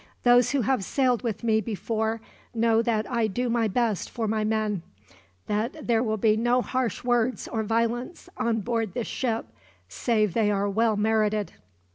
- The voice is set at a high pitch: Yes, high, 225 Hz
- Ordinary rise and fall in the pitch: No, narrow, 1.9 semitones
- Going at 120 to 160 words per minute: No, average, 170 wpm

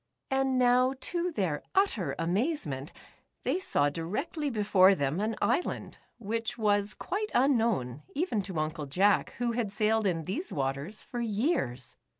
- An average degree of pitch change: No, wide, 7.4 semitones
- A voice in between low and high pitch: No, high, 215 Hz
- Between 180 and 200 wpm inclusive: No, average, 150 wpm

